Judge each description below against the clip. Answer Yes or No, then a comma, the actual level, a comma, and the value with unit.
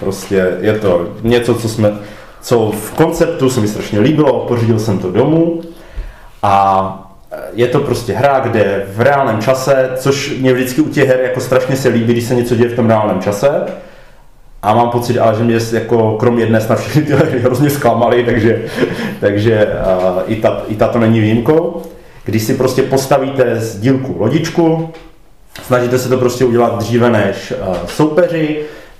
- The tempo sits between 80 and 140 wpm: No, fast, 170 wpm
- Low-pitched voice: Yes, low, 120 Hz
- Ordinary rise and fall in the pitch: Yes, average, 3.6 semitones